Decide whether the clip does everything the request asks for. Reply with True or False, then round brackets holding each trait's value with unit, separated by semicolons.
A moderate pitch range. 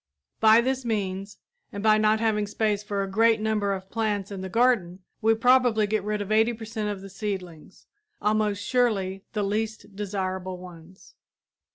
False (2.2 semitones)